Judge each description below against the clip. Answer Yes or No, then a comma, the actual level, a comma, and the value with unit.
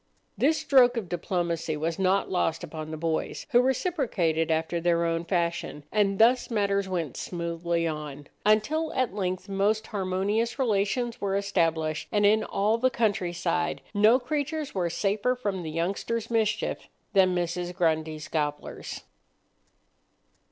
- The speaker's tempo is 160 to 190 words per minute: No, slow, 135 wpm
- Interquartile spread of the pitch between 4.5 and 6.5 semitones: Yes, average, 4.8 semitones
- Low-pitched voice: No, high, 190 Hz